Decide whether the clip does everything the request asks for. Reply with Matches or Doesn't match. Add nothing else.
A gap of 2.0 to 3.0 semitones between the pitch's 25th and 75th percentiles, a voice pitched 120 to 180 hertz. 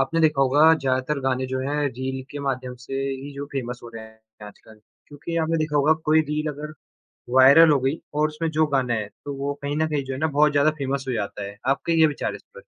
Matches